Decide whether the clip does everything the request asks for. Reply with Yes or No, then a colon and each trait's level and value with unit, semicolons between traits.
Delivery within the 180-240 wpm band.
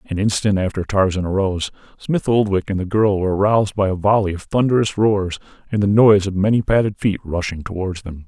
Yes: fast, 205 wpm